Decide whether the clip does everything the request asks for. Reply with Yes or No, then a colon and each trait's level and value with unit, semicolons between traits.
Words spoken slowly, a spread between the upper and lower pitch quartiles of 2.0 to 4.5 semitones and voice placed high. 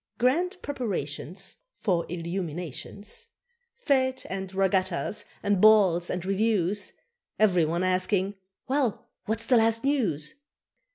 Yes: slow, 105 wpm; average, 4.2 semitones; high, 195 Hz